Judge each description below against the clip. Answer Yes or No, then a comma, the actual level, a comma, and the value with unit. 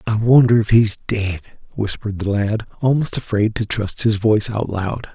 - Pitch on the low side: Yes, low, 110 Hz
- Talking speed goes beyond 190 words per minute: No, average, 185 wpm